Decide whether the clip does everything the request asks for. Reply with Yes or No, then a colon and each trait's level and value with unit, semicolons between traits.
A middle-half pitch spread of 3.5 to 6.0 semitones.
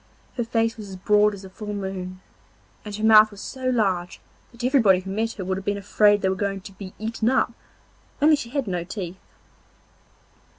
No: average, 3.0 semitones